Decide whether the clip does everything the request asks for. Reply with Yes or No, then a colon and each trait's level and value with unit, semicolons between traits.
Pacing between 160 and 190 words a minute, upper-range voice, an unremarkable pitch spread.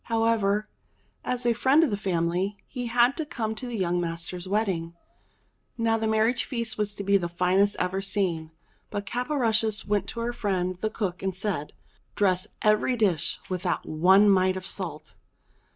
Yes: average, 170 wpm; high, 200 Hz; average, 3.6 semitones